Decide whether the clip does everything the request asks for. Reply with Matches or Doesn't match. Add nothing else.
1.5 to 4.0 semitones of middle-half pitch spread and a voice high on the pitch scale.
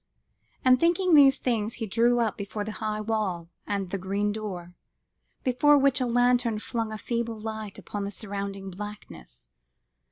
Matches